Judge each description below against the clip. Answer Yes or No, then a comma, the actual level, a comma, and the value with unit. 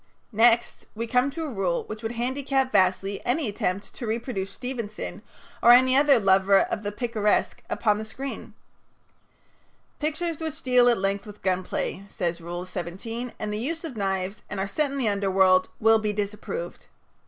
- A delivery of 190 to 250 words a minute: No, average, 175 wpm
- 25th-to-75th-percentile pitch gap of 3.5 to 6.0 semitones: Yes, average, 4.7 semitones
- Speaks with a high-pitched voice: Yes, high, 220 Hz